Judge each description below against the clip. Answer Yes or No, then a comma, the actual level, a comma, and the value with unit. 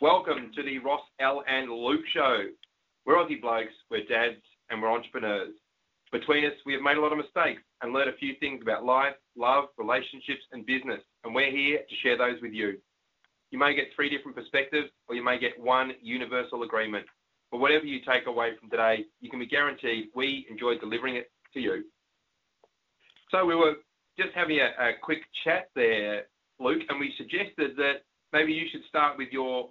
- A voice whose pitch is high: No, medium, 140 Hz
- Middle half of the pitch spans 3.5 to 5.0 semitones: No, average, 3.1 semitones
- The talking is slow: No, average, 190 wpm